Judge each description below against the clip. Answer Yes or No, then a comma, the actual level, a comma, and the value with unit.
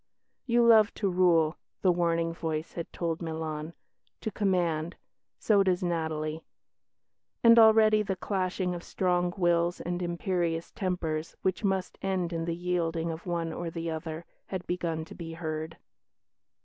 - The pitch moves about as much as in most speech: No, narrow, 2.1 semitones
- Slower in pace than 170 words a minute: Yes, average, 150 wpm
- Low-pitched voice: No, medium, 175 Hz